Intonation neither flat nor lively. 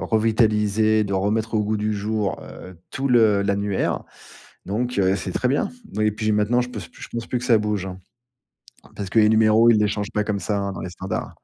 No: narrow, 1.7 semitones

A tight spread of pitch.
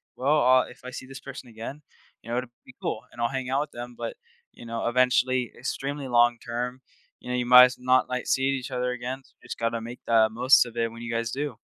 Yes: narrow, 1.7 semitones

